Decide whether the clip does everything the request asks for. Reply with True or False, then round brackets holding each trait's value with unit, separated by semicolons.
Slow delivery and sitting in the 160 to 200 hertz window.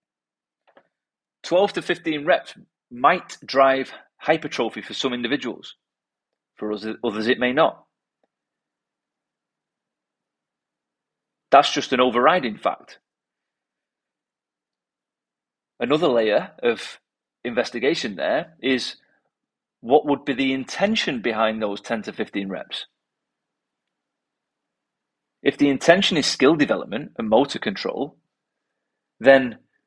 False (95 wpm; 130 Hz)